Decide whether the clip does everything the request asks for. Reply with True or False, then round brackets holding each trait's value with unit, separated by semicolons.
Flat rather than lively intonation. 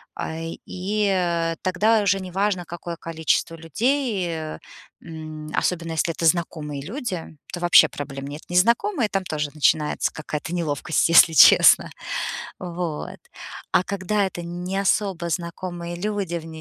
False (3.0 semitones)